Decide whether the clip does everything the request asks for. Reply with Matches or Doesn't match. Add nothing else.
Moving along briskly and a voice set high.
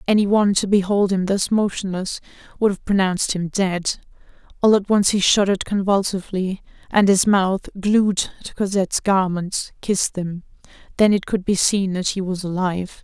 Doesn't match